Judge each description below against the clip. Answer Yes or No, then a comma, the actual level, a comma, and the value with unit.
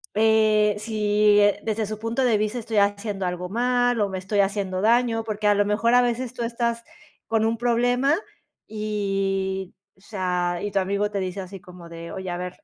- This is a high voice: Yes, high, 210 Hz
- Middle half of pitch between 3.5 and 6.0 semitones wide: No, average, 2.8 semitones